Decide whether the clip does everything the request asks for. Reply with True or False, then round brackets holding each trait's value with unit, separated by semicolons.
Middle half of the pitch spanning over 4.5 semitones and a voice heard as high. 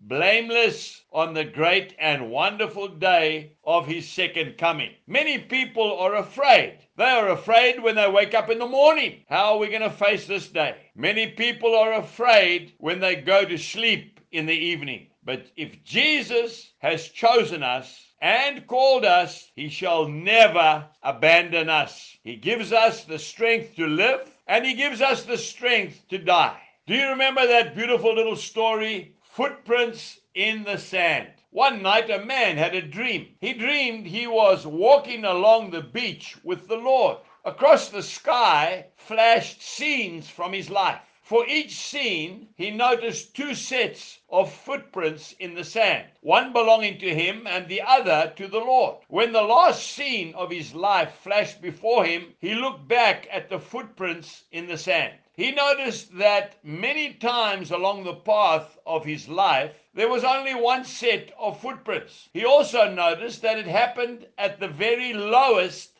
True (5.6 semitones; 215 Hz)